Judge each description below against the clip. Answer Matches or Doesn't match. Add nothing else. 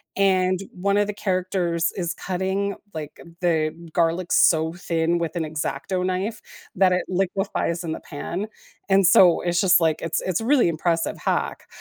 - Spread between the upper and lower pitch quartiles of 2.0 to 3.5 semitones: Matches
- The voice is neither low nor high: Matches